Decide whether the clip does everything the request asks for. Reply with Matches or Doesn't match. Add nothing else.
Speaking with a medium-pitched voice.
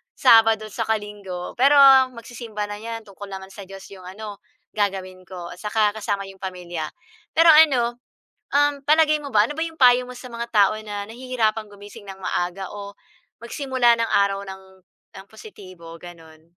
Doesn't match